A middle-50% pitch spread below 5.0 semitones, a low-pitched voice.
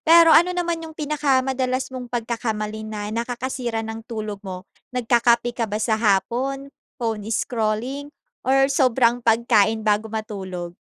No: average, 3.2 semitones; high, 235 Hz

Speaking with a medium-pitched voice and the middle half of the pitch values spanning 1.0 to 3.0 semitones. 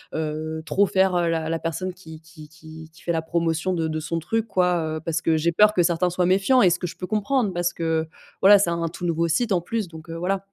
Yes: medium, 170 Hz; narrow, 2.5 semitones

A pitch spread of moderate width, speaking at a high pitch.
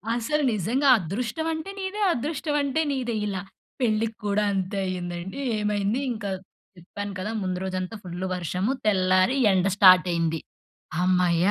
Yes: average, 4.5 semitones; high, 200 Hz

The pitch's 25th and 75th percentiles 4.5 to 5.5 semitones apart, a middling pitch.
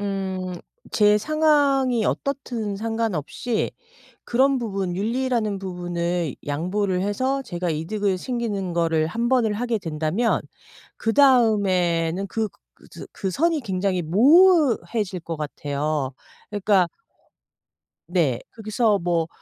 No: average, 5.2 semitones; high, 200 Hz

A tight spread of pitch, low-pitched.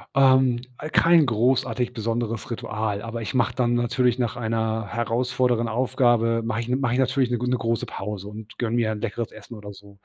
Yes: narrow, 2.0 semitones; low, 115 Hz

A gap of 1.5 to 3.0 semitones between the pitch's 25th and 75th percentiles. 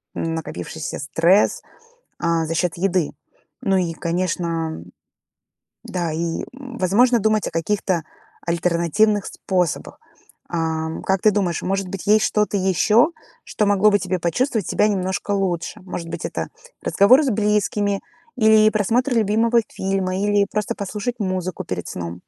No: average, 3.8 semitones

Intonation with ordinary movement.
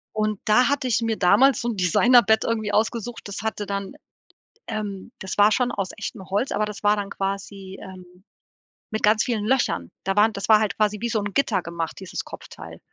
No: narrow, 2.3 semitones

